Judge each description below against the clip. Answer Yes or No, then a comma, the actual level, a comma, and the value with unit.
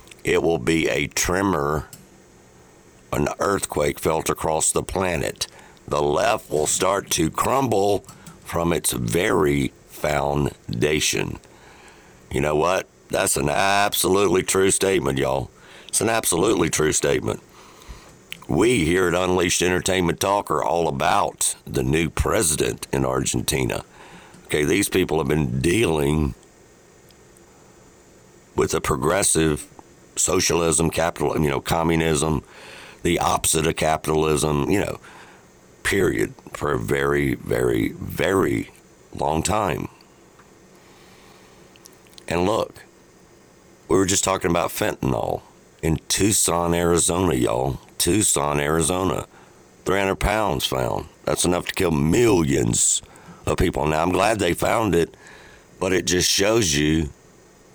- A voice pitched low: Yes, very low, 80 Hz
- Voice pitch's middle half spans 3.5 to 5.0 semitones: Yes, average, 4.1 semitones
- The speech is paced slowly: Yes, slow, 115 wpm